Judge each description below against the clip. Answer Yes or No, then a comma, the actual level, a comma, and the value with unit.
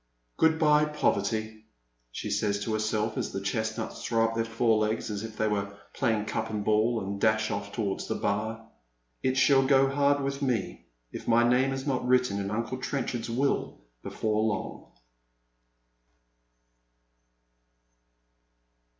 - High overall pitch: No, low, 115 Hz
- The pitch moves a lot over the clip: No, average, 3.3 semitones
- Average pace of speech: Yes, average, 150 wpm